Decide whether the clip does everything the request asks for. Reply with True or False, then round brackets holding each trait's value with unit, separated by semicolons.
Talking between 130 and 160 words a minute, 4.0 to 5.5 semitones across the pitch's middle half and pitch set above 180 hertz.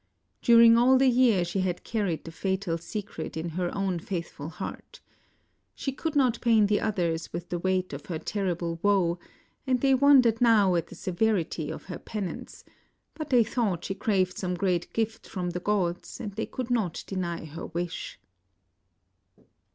False (170 wpm; 4.7 semitones; 190 Hz)